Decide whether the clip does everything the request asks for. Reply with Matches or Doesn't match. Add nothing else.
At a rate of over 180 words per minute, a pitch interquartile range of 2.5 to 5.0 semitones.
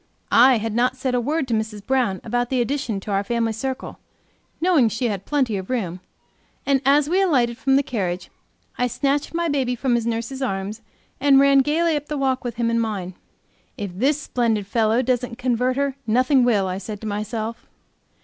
Matches